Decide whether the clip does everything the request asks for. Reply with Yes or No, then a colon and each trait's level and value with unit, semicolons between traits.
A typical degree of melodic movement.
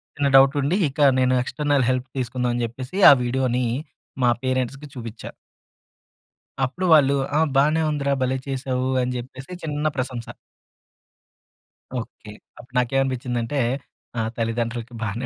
No: narrow, 2.1 semitones